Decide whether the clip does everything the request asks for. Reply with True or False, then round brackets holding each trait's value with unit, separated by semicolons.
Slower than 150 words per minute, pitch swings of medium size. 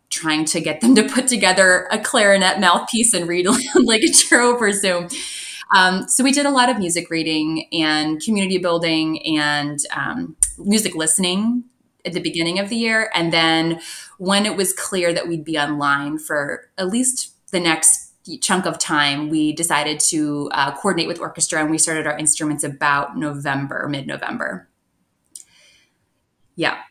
False (165 wpm; 4.6 semitones)